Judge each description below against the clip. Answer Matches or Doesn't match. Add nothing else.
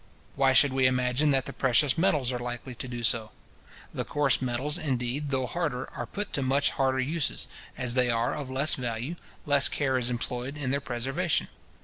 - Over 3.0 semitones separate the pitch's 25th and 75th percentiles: Doesn't match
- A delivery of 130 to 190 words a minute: Doesn't match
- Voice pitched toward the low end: Matches